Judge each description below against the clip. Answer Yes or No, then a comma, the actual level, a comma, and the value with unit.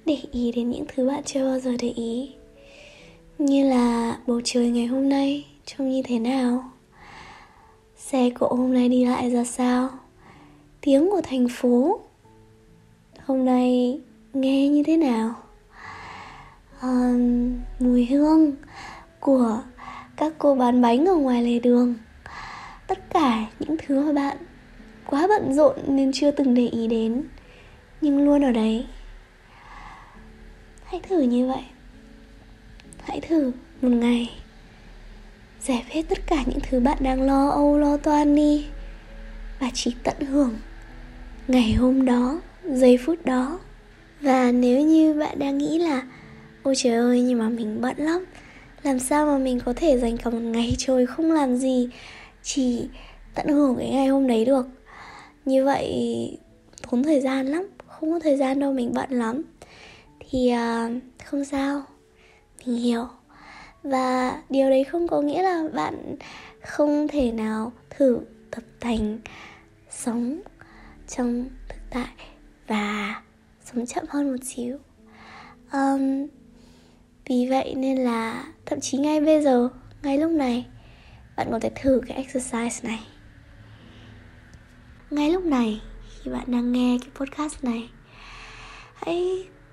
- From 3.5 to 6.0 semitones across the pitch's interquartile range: No, average, 2.9 semitones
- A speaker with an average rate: No, slow, 145 wpm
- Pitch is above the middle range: Yes, very high, 260 Hz